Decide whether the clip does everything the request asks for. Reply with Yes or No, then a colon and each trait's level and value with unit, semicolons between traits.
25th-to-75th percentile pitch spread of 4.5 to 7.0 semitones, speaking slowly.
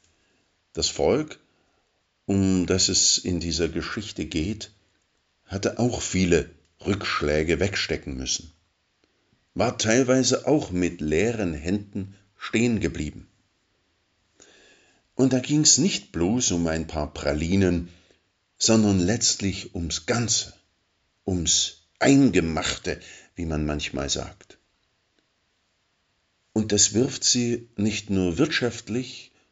Yes: wide, 5.4 semitones; slow, 100 wpm